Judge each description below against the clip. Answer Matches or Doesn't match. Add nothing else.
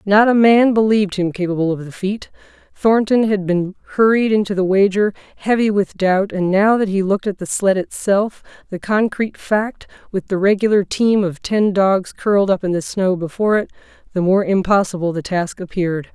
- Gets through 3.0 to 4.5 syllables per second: Doesn't match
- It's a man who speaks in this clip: Doesn't match